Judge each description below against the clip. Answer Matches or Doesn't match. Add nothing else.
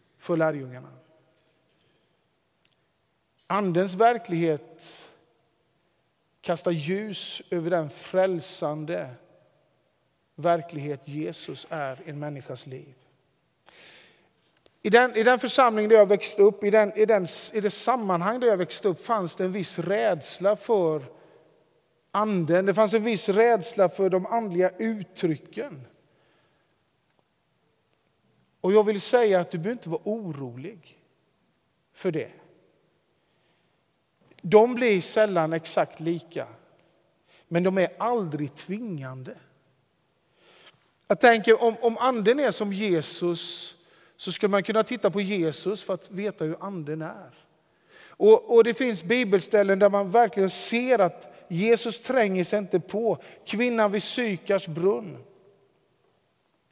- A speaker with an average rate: Doesn't match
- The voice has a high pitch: Matches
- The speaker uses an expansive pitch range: Doesn't match